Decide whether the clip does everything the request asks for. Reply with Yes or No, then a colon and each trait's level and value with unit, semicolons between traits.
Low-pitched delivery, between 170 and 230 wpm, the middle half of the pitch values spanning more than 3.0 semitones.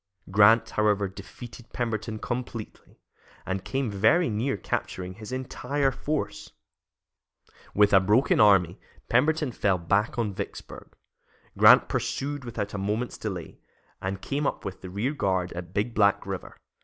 No: low, 105 Hz; average, 140 wpm; average, 4.1 semitones